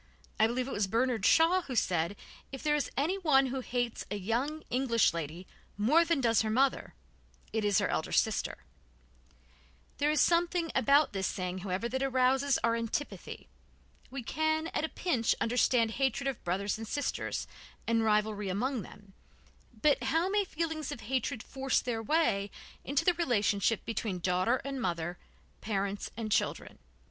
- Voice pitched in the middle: No, high, 245 Hz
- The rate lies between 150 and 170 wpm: Yes, average, 160 wpm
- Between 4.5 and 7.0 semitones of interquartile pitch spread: Yes, wide, 5.4 semitones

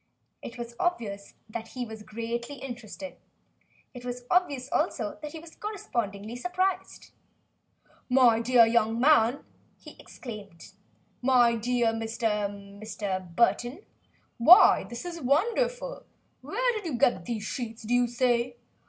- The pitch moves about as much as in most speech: Yes, average, 4.2 semitones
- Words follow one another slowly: Yes, slow, 130 wpm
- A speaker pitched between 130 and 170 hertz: No, high, 240 Hz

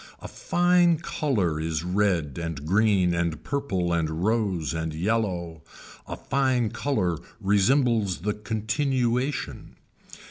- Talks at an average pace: No, slow, 110 wpm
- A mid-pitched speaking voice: No, low, 100 Hz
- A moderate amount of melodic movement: No, wide, 6.5 semitones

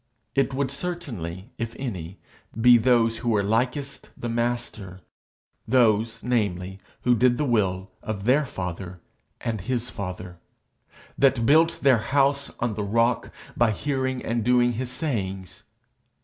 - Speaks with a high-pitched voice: No, low, 115 Hz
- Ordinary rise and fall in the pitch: Yes, average, 4.3 semitones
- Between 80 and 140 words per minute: Yes, slow, 135 wpm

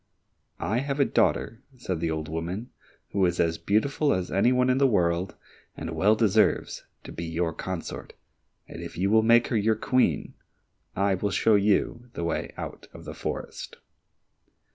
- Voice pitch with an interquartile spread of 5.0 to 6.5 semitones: Yes, average, 5.3 semitones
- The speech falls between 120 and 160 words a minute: No, average, 175 wpm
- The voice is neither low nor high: No, low, 100 Hz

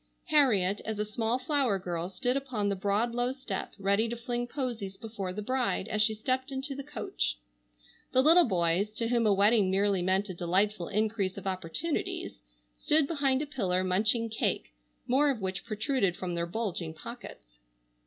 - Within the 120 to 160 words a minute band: No, average, 175 wpm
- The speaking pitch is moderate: No, high, 215 Hz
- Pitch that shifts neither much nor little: Yes, average, 5.0 semitones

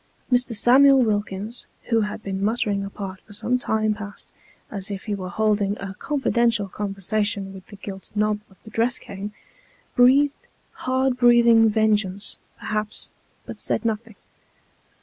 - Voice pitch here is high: Yes, high, 215 Hz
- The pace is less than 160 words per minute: Yes, average, 145 wpm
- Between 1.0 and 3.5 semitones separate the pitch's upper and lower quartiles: Yes, average, 2.9 semitones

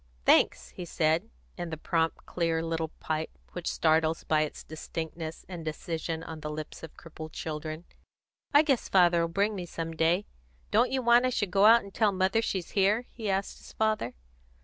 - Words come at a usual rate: Yes, average, 185 wpm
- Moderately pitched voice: Yes, medium, 170 Hz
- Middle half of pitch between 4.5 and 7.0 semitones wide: No, average, 3.8 semitones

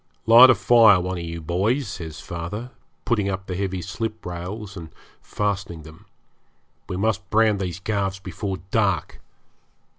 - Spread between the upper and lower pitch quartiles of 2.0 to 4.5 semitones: Yes, average, 3.5 semitones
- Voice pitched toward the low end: Yes, very low, 95 Hz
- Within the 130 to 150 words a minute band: Yes, average, 145 wpm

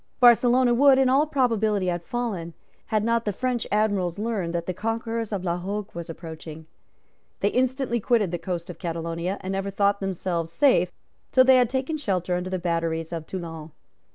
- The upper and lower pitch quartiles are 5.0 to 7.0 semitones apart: Yes, wide, 5.6 semitones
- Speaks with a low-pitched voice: No, high, 195 Hz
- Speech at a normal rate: Yes, average, 180 wpm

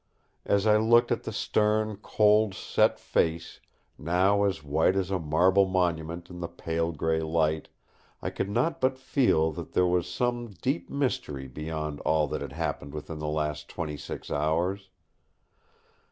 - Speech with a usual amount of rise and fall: Yes, average, 4.8 semitones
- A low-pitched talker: Yes, very low, 90 Hz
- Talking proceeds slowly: No, average, 160 wpm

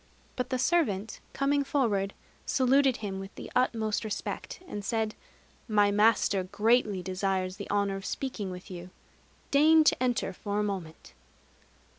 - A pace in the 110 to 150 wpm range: Yes, average, 145 wpm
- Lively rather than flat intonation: No, average, 4.6 semitones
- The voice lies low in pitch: No, high, 210 Hz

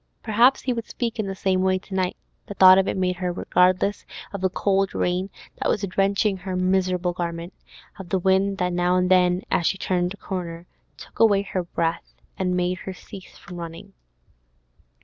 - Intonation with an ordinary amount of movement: No, narrow, 1.5 semitones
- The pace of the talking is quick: No, average, 195 wpm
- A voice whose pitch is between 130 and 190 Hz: Yes, medium, 185 Hz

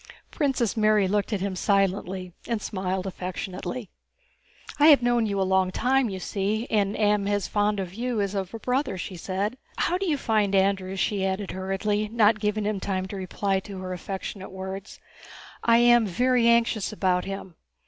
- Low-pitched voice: No, high, 200 Hz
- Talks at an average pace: Yes, average, 180 wpm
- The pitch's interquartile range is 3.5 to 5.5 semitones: No, average, 2.7 semitones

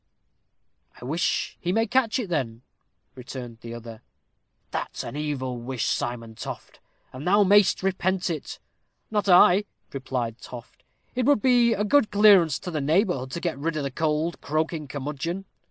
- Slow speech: No, average, 160 wpm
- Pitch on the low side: No, medium, 155 Hz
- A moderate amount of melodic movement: No, wide, 6.8 semitones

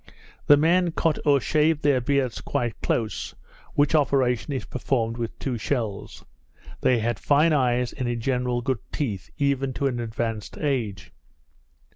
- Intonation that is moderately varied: Yes, average, 3.4 semitones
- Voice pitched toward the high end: No, low, 130 Hz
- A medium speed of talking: Yes, average, 150 wpm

